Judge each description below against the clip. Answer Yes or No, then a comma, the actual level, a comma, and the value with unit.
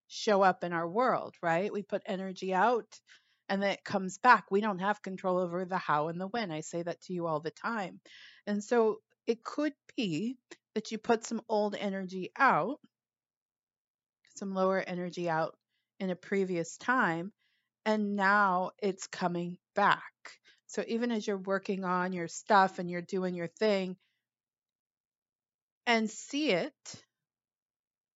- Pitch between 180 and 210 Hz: Yes, high, 190 Hz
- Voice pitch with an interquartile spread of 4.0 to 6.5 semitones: No, average, 3.2 semitones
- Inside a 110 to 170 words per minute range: Yes, average, 160 wpm